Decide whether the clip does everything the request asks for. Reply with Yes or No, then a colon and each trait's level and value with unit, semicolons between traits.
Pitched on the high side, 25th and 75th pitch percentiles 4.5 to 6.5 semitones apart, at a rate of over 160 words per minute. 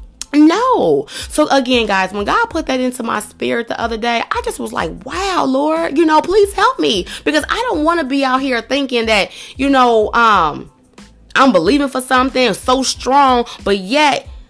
Yes: very high, 270 Hz; average, 5.3 semitones; average, 190 wpm